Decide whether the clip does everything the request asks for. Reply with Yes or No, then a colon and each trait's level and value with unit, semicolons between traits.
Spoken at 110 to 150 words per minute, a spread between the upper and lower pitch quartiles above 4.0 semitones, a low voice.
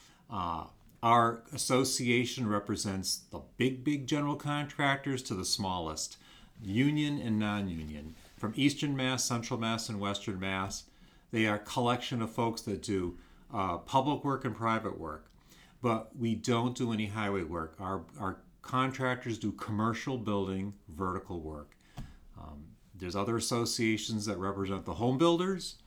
Yes: average, 140 wpm; average, 4.7 semitones; low, 110 Hz